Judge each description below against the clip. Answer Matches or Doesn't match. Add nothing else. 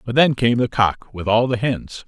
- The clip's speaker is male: Matches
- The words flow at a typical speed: Doesn't match